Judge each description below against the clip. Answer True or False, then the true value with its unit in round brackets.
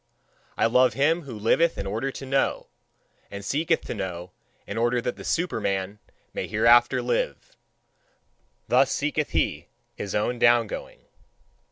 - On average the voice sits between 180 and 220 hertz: False (120 Hz)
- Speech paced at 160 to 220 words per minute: False (145 wpm)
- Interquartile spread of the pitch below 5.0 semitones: True (4.6 semitones)